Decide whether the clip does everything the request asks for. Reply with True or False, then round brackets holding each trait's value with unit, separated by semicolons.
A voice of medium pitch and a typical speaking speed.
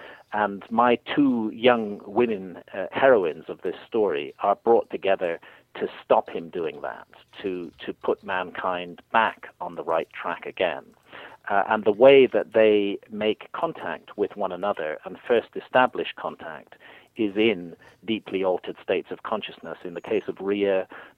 False (110 Hz; 155 wpm)